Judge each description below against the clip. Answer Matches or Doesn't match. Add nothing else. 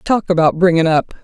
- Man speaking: Doesn't match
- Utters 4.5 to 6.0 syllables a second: Matches